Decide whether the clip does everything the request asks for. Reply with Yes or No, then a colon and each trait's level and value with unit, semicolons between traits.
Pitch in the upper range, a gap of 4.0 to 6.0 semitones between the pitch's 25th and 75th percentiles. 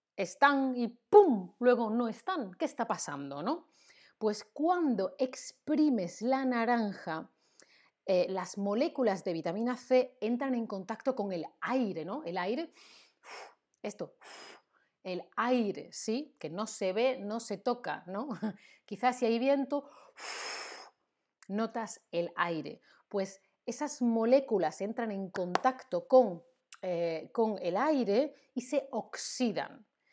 Yes: high, 230 Hz; average, 4.7 semitones